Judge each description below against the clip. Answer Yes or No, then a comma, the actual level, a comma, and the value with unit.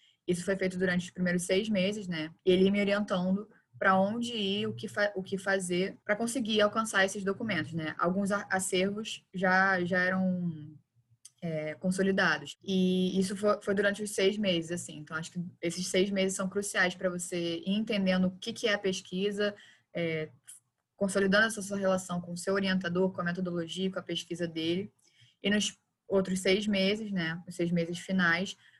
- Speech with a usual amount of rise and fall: No, narrow, 2.3 semitones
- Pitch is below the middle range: No, high, 190 Hz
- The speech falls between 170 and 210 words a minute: Yes, average, 180 wpm